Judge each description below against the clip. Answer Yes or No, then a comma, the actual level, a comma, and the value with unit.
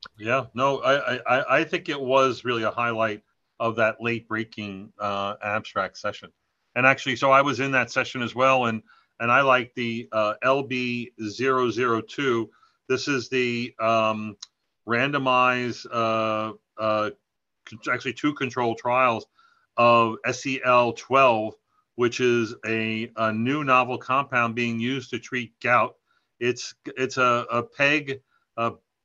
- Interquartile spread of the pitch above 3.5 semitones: No, narrow, 2.6 semitones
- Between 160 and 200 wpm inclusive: No, average, 140 wpm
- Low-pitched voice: Yes, low, 120 Hz